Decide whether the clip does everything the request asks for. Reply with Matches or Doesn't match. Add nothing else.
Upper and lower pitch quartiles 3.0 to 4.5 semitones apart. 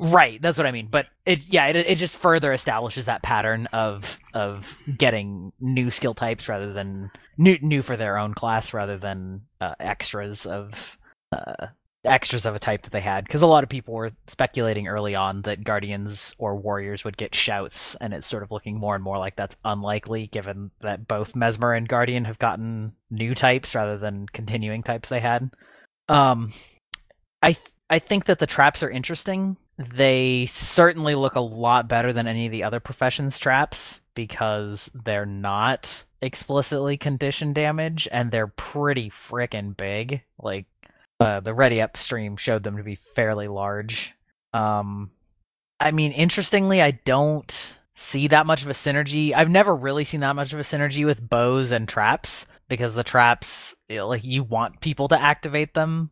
Doesn't match